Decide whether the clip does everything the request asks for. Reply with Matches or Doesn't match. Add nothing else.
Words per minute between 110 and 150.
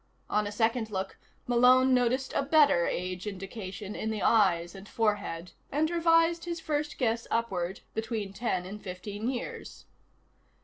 Matches